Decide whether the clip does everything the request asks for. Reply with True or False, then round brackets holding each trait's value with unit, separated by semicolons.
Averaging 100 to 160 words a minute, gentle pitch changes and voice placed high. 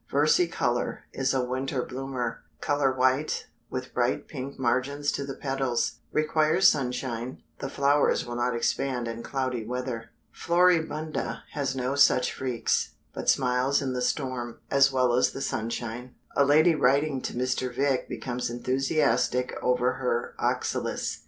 False (140 wpm; 2.1 semitones; 130 Hz)